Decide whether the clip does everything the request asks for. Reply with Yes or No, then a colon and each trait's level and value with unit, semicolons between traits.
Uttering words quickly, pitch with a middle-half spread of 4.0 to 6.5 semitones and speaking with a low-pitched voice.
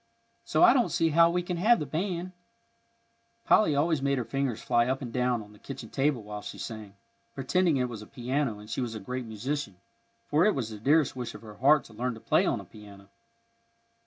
Yes: fast, 225 wpm; wide, 5.4 semitones; low, 130 Hz